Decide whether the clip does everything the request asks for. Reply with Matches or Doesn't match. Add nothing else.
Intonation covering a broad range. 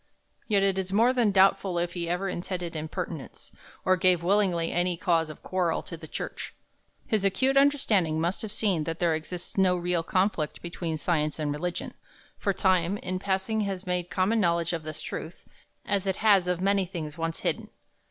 Doesn't match